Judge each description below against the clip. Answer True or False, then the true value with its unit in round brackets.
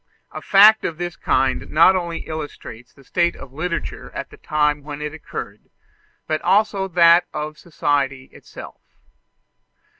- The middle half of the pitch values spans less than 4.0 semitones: True (3.1 semitones)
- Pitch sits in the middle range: True (155 Hz)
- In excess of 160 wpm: False (145 wpm)